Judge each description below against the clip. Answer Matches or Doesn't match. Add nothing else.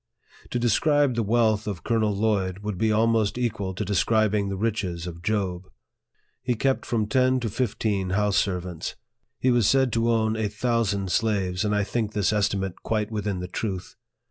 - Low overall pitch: Matches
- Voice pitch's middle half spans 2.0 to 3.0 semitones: Matches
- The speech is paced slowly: Doesn't match